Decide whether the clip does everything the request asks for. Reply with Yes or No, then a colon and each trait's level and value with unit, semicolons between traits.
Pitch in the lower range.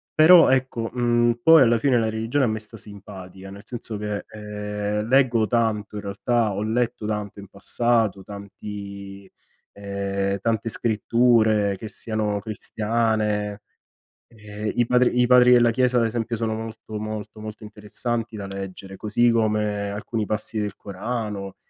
Yes: low, 110 Hz